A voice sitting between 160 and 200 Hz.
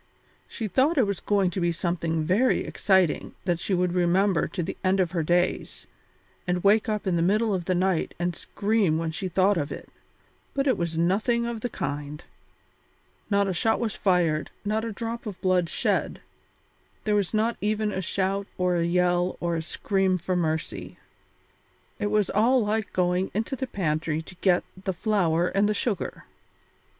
Yes: medium, 185 Hz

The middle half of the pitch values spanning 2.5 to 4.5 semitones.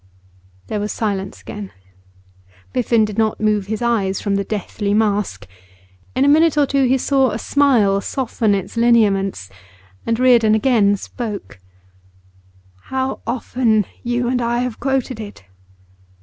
Yes: average, 3.6 semitones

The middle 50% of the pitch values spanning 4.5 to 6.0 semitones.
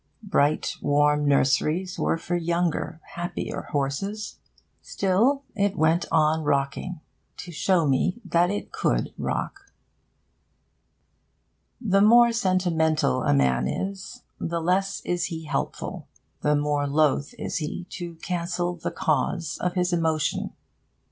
No: average, 3.8 semitones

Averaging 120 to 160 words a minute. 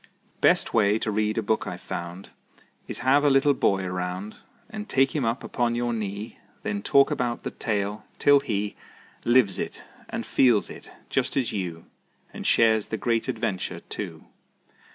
No: average, 170 wpm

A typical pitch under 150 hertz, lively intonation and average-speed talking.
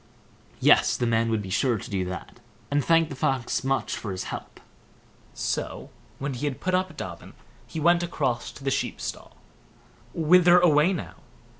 Yes: medium, 140 Hz; wide, 6.3 semitones; average, 175 wpm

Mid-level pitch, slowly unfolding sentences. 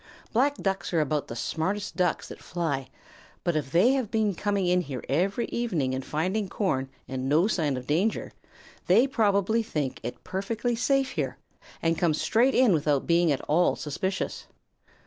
No: medium, 180 Hz; average, 170 wpm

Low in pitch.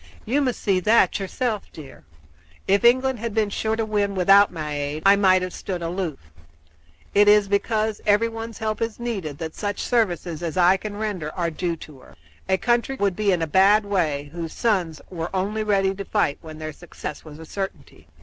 No: high, 195 Hz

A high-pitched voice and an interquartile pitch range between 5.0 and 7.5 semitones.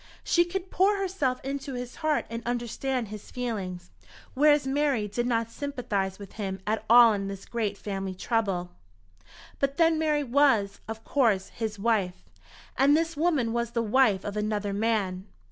Yes: high, 235 Hz; average, 5.3 semitones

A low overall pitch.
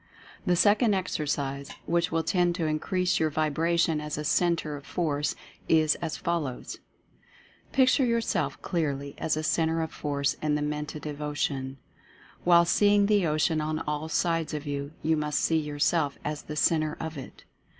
No: medium, 155 Hz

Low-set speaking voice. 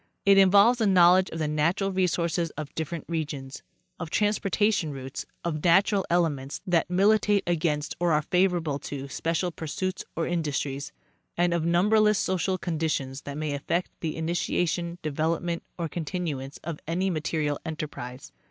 No: medium, 170 Hz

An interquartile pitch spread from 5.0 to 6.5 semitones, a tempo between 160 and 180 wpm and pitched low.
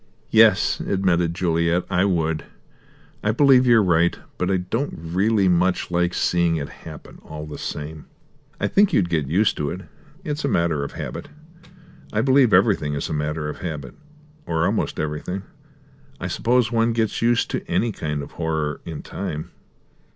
Yes: wide, 5.6 semitones; average, 165 wpm; very low, 90 Hz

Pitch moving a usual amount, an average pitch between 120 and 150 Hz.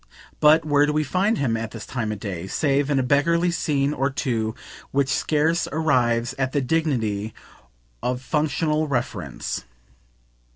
Yes: average, 4.5 semitones; medium, 140 Hz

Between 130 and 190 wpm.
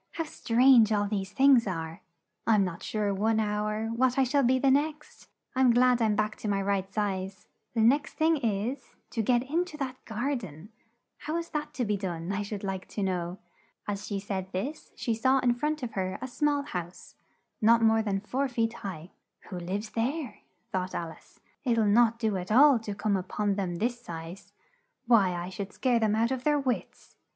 No: fast, 205 wpm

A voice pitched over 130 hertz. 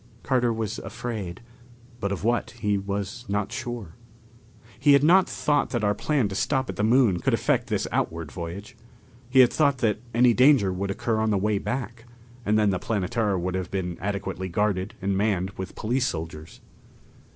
No: low, 105 Hz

